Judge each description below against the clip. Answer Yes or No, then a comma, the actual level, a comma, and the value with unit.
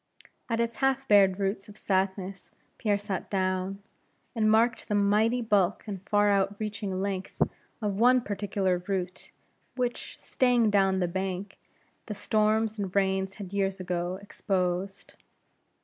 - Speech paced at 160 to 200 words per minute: No, average, 140 wpm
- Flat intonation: Yes, narrow, 2.2 semitones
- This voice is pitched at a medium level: No, high, 200 Hz